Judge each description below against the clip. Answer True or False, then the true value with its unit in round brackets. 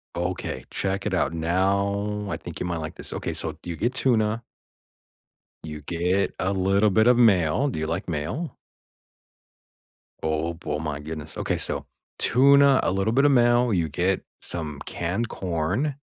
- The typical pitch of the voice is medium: False (95 Hz)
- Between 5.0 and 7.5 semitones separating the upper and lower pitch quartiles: True (5.4 semitones)